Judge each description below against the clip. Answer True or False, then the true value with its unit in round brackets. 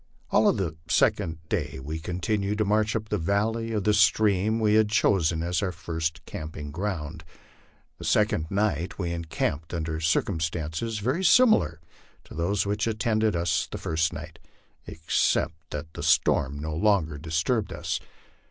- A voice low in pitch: True (90 Hz)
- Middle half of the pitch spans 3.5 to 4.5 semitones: False (4.9 semitones)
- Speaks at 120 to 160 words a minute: True (155 wpm)